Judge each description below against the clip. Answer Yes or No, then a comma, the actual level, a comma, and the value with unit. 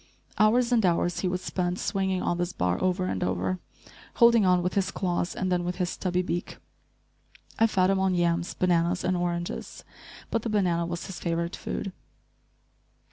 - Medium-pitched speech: Yes, medium, 180 Hz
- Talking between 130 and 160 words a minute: No, average, 180 wpm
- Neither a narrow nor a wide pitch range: No, narrow, 1.7 semitones